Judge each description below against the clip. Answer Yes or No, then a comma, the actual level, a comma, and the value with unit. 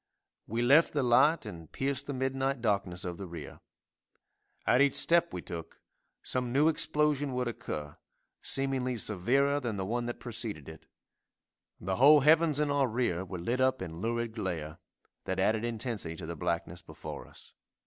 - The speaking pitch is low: Yes, low, 120 Hz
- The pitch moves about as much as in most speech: No, wide, 6.4 semitones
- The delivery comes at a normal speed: Yes, average, 170 wpm